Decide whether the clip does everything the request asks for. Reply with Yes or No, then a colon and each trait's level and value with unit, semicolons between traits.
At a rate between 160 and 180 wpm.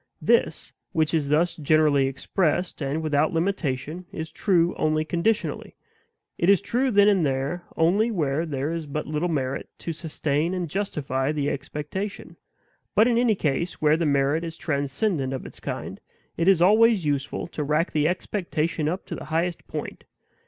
Yes: average, 165 wpm